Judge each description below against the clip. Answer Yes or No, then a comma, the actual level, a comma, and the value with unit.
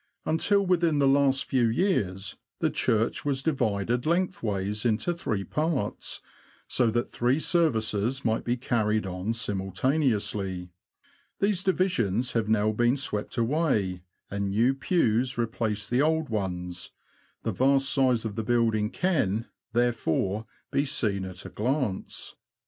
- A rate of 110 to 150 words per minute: Yes, slow, 135 wpm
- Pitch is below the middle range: Yes, low, 115 Hz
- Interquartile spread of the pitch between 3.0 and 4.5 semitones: No, average, 5.0 semitones